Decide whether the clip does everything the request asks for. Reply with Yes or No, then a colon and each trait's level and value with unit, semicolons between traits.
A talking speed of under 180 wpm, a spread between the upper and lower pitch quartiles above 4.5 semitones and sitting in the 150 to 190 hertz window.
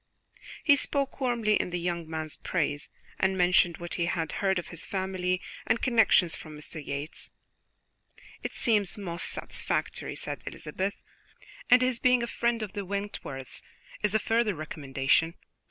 Yes: average, 155 wpm; average, 5.1 semitones; medium, 185 Hz